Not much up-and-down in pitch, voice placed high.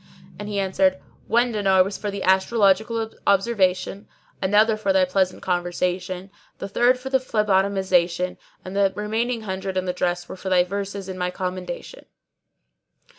Yes: narrow, 2.2 semitones; high, 195 Hz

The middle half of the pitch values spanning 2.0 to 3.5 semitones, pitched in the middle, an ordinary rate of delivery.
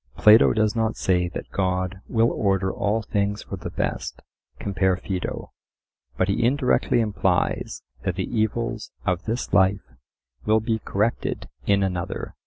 No: average, 2.8 semitones; low, 100 Hz; average, 145 wpm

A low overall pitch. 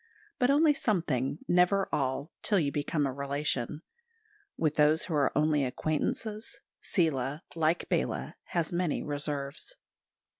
No: medium, 155 Hz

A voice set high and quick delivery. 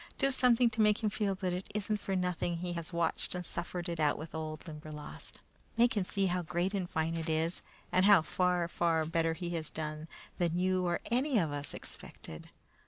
No: medium, 175 Hz; fast, 215 wpm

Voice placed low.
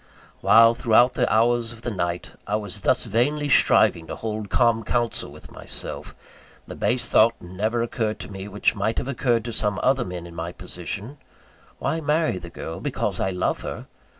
Yes: low, 110 Hz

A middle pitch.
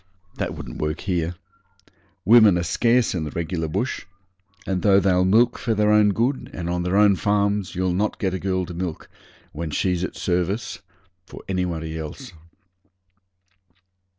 No: very low, 95 Hz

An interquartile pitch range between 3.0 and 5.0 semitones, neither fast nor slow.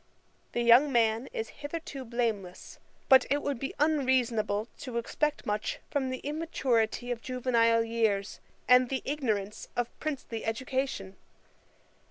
No: average, 3.3 semitones; slow, 130 wpm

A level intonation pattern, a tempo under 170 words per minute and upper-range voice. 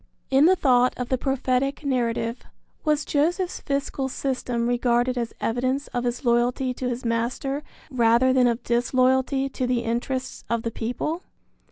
Yes: narrow, 2.1 semitones; average, 155 wpm; very high, 255 Hz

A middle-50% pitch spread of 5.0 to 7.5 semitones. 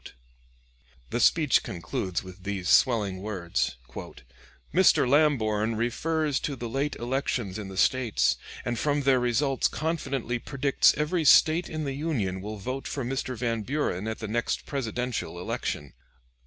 Yes: wide, 5.6 semitones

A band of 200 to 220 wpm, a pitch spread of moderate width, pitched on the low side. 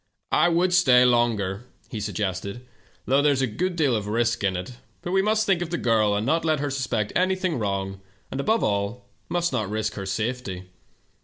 No: fast, 205 wpm; wide, 7.9 semitones; low, 120 Hz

